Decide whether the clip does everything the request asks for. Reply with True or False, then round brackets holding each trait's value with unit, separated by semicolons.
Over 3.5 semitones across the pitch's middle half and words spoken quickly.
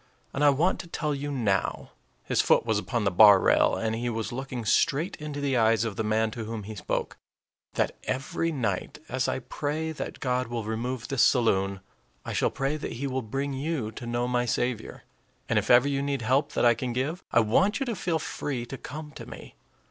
True (4.1 semitones; 220 wpm)